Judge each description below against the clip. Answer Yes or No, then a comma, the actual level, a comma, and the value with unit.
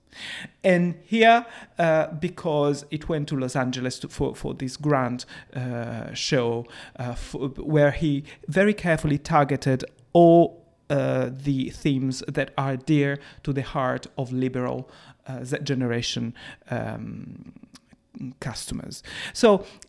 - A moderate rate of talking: No, slow, 120 wpm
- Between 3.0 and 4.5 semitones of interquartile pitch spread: Yes, average, 3.6 semitones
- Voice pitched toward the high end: No, medium, 140 Hz